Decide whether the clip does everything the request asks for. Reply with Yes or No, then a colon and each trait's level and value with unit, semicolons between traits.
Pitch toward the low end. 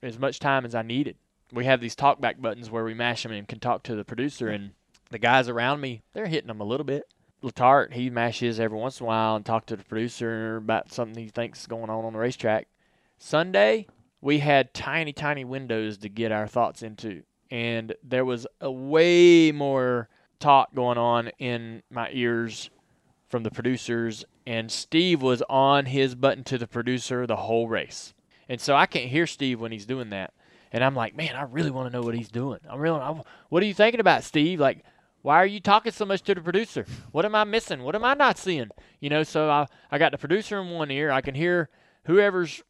Yes: low, 125 Hz